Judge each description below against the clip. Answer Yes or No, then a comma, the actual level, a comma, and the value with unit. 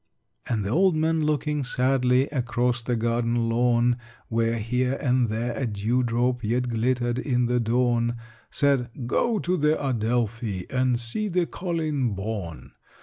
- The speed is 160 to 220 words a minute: No, average, 150 wpm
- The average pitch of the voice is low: Yes, low, 125 Hz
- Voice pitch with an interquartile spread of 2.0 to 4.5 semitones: Yes, narrow, 2.4 semitones